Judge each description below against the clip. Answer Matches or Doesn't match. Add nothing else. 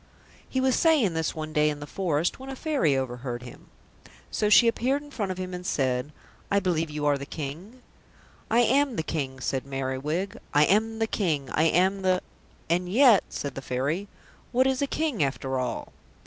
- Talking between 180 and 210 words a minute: Matches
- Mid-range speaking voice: Matches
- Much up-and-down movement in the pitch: Matches